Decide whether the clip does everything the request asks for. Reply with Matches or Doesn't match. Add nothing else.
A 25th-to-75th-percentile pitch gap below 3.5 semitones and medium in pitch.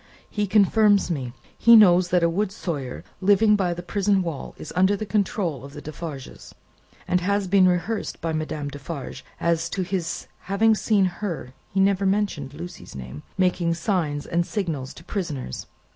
Doesn't match